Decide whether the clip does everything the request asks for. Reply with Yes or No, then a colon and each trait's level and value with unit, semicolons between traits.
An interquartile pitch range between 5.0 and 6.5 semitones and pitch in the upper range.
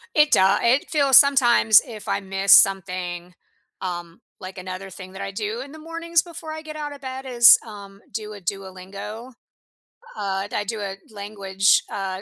Yes: average, 5.3 semitones; high, 205 Hz